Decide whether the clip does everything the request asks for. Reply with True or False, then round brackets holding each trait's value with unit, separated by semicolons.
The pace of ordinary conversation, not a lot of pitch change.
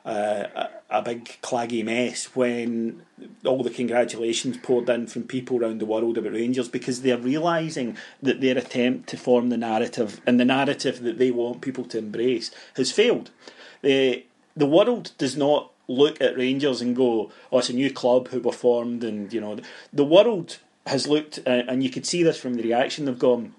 True (190 wpm; 1.9 semitones)